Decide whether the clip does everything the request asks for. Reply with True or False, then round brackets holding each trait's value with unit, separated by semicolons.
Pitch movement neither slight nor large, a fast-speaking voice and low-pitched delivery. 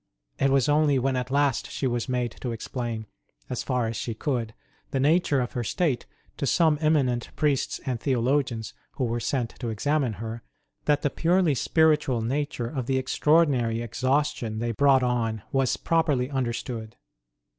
False (3.5 semitones; 165 wpm; 130 Hz)